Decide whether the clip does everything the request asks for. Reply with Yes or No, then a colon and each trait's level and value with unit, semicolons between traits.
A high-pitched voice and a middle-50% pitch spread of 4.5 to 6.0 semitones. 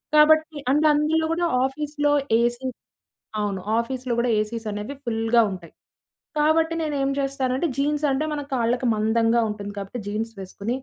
Yes: very high, 255 Hz; average, 4.8 semitones